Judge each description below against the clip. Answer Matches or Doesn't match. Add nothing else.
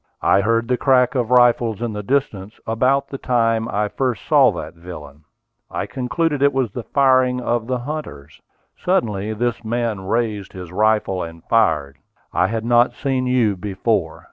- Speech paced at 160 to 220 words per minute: Matches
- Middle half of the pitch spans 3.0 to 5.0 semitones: Matches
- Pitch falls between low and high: Doesn't match